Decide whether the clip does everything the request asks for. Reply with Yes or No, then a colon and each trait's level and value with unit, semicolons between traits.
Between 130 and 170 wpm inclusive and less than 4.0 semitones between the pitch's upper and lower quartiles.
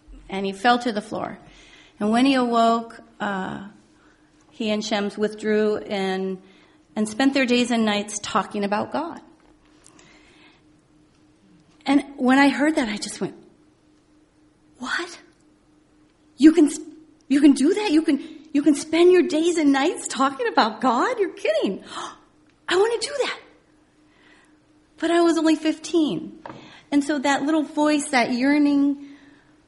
No: average, 145 wpm; average, 5.0 semitones